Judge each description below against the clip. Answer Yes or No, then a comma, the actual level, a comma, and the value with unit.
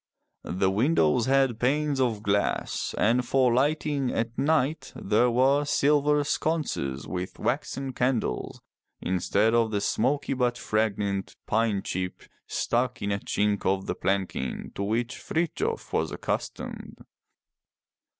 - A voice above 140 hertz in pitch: No, low, 120 Hz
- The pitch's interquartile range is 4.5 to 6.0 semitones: Yes, average, 5.2 semitones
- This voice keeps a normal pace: No, slow, 125 wpm